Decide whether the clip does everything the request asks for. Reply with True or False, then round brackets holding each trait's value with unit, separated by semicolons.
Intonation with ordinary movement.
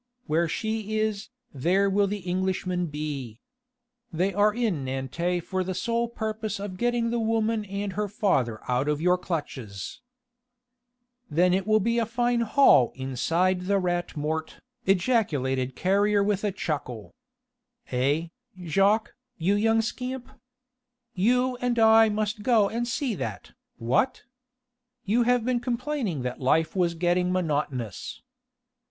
False (5.7 semitones)